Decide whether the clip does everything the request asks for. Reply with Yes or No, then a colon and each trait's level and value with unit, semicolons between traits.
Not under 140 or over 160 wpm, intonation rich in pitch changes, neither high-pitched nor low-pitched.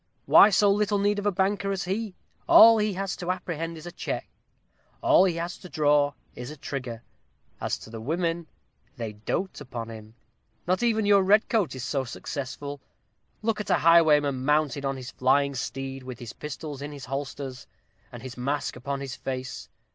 No: average, 185 wpm; wide, 6.2 semitones; medium, 150 Hz